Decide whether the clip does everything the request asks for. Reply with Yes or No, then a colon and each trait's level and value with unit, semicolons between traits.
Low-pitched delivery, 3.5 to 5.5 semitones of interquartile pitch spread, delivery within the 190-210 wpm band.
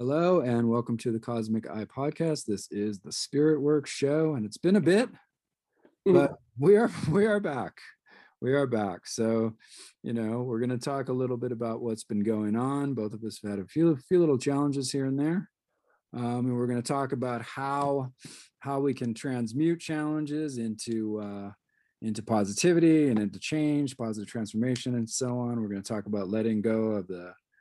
Yes: low, 125 Hz; average, 4.5 semitones; average, 200 wpm